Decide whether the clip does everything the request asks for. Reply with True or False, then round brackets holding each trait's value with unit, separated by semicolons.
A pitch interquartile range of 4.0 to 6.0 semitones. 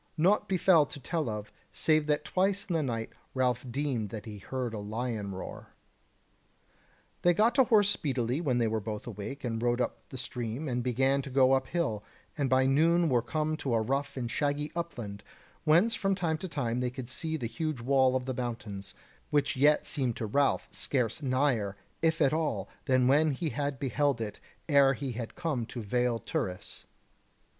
True (4.5 semitones)